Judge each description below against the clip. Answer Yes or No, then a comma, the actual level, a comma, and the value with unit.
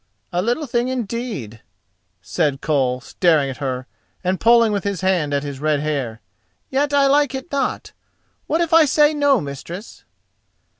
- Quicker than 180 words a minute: No, average, 160 wpm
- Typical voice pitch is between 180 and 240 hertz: Yes, high, 190 Hz